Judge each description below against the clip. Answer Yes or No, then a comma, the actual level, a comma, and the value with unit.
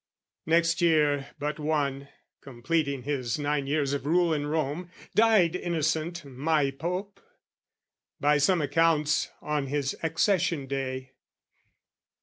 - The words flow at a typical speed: No, slow, 115 wpm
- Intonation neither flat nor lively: Yes, average, 3.0 semitones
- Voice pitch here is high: No, medium, 150 Hz